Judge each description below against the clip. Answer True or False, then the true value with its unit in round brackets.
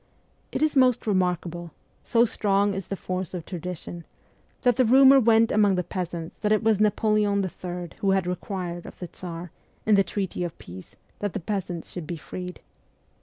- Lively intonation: False (3.3 semitones)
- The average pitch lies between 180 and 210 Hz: True (190 Hz)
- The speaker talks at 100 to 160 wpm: False (180 wpm)